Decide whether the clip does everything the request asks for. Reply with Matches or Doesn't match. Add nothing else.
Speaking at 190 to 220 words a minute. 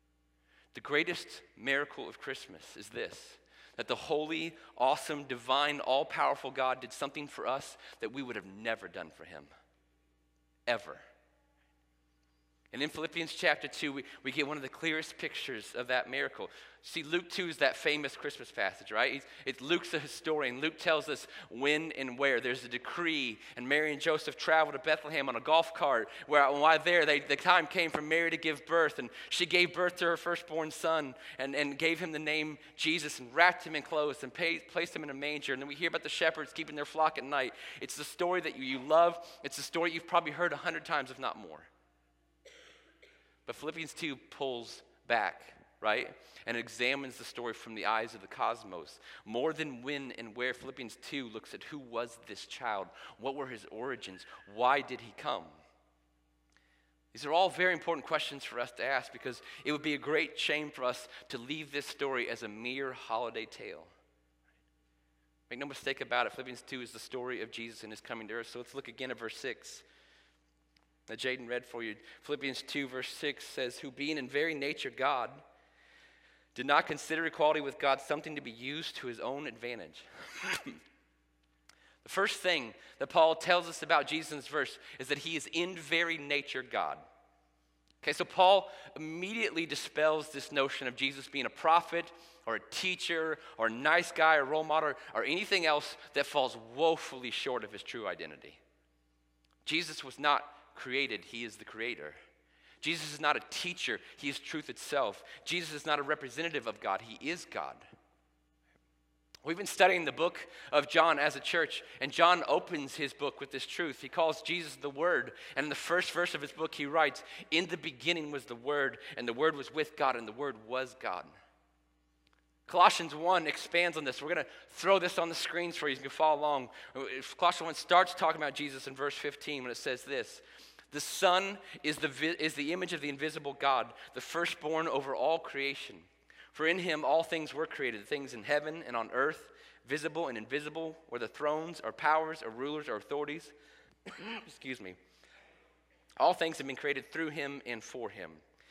Matches